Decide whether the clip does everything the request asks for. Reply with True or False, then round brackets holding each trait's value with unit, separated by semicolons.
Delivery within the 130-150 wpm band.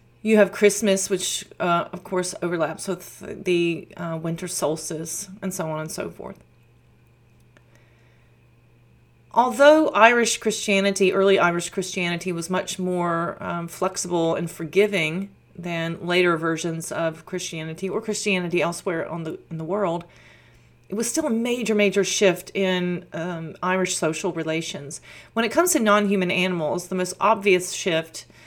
True (140 wpm)